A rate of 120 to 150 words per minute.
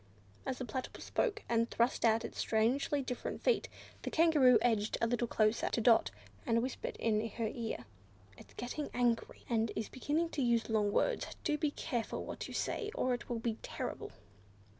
No: average, 185 wpm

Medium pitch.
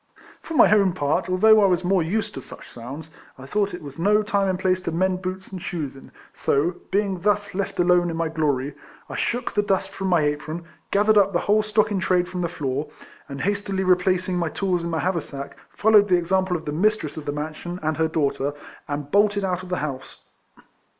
Yes: medium, 180 Hz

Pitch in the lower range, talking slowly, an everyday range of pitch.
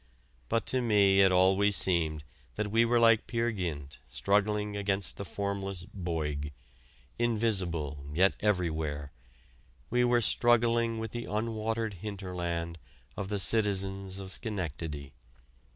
Yes: low, 100 Hz; slow, 120 wpm; average, 4.3 semitones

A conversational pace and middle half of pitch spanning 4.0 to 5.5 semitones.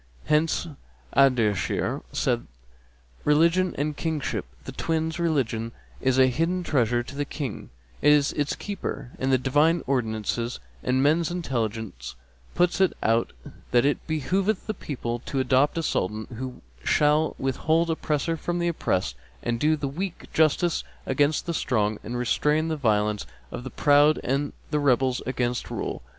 Yes: average, 145 wpm; average, 4.6 semitones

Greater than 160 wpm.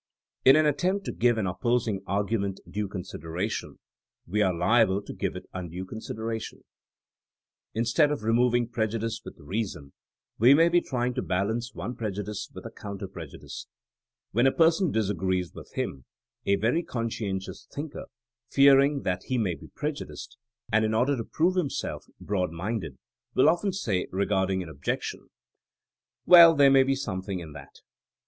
No: average, 155 wpm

